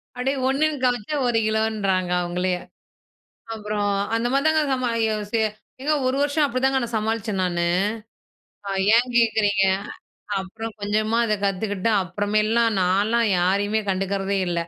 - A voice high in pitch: Yes, high, 215 Hz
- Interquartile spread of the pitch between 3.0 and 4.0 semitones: Yes, average, 3.4 semitones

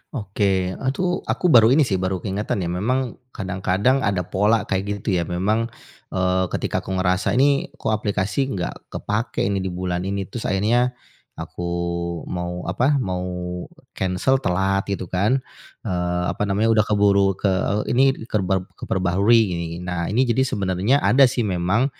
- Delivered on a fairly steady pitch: No, average, 3.8 semitones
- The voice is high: No, low, 100 Hz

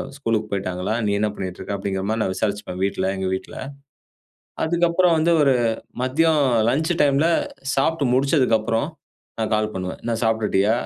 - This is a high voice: No, low, 115 Hz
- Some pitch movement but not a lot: No, wide, 6.1 semitones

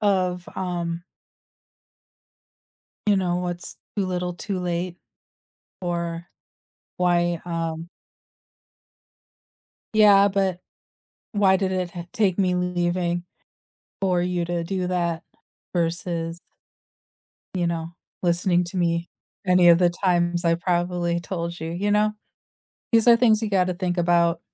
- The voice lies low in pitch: No, medium, 175 Hz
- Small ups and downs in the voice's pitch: Yes, narrow, 1.4 semitones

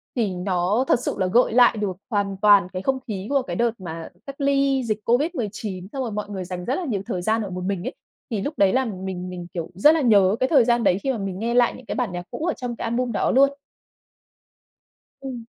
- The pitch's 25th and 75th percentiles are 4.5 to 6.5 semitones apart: Yes, average, 5.1 semitones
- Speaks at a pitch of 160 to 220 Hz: Yes, high, 215 Hz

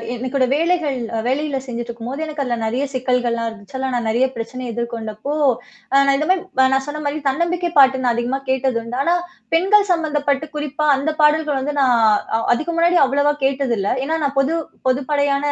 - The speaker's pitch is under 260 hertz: No, very high, 275 Hz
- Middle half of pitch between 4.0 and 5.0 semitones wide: No, average, 3.6 semitones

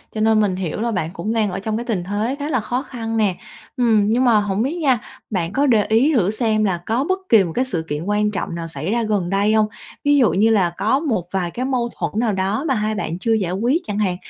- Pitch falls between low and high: No, high, 215 Hz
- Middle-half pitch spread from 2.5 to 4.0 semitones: Yes, average, 3.7 semitones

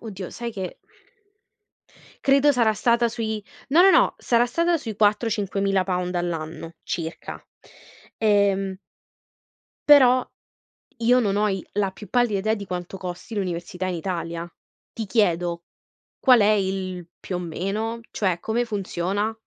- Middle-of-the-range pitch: No, high, 200 Hz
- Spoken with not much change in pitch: No, average, 4.0 semitones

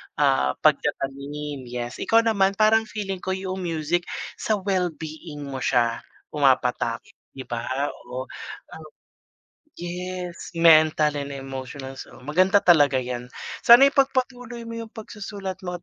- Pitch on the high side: No, medium, 165 Hz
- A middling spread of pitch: No, wide, 6.3 semitones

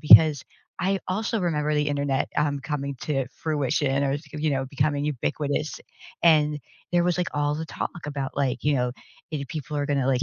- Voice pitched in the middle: Yes, medium, 145 Hz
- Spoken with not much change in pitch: Yes, narrow, 1.8 semitones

